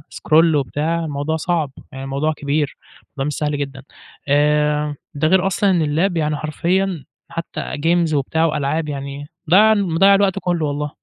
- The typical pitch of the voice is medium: Yes, medium, 155 Hz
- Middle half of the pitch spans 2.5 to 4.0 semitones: Yes, average, 2.9 semitones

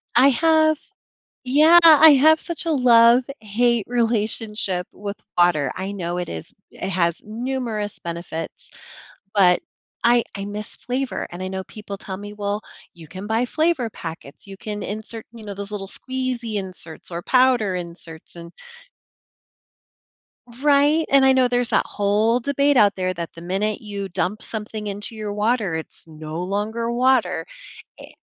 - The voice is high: Yes, high, 210 Hz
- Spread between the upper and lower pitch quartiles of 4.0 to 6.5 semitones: Yes, average, 4.8 semitones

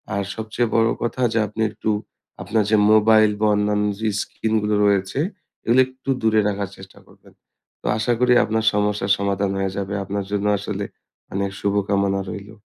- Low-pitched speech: Yes, low, 105 Hz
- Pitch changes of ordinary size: No, narrow, 1.9 semitones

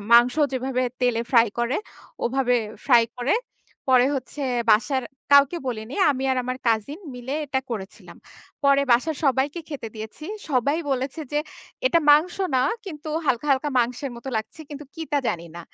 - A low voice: No, very high, 260 Hz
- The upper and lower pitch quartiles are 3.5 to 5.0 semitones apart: No, average, 3.0 semitones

